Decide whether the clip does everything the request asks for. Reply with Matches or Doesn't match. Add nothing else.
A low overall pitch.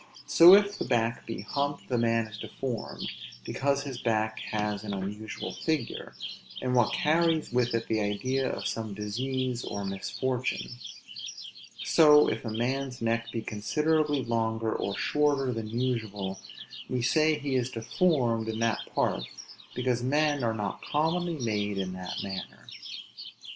Matches